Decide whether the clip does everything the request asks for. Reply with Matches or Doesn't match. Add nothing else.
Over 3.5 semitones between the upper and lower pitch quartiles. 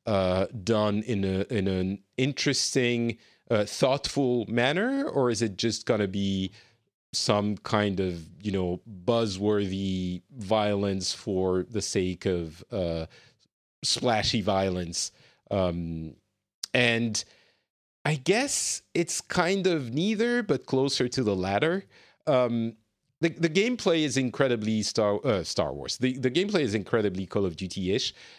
Matches